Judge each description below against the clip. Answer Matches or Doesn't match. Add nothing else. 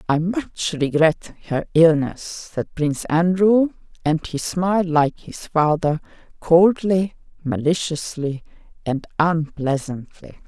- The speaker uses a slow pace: Matches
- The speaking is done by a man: Doesn't match